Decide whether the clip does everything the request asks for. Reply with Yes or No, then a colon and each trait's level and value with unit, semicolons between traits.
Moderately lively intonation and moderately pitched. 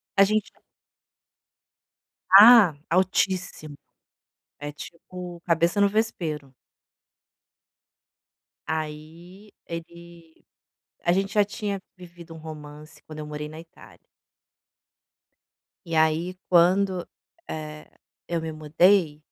Yes: average, 3.3 semitones; medium, 170 Hz